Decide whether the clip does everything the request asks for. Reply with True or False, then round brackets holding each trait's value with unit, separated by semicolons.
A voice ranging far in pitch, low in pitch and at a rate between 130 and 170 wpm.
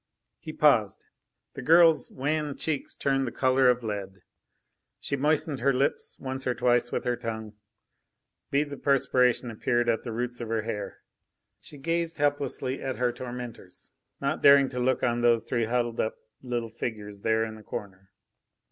False (3.1 semitones; 125 Hz; 165 wpm)